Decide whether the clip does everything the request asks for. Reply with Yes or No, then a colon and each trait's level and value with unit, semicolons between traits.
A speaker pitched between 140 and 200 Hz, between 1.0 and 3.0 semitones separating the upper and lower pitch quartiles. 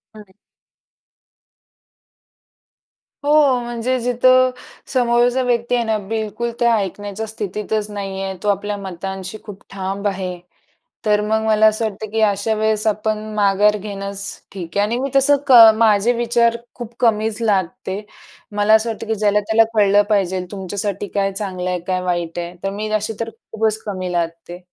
No: high, 210 Hz; narrow, 2.5 semitones